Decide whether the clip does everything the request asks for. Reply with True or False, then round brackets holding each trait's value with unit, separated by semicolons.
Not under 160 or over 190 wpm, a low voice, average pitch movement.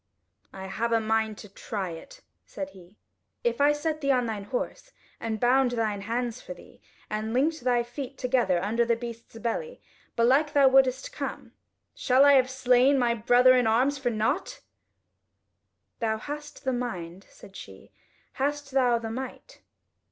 False (165 wpm; 245 Hz; 3.6 semitones)